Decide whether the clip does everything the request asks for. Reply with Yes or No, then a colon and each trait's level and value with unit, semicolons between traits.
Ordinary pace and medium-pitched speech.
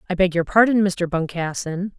Yes: average, 180 wpm; medium, 180 Hz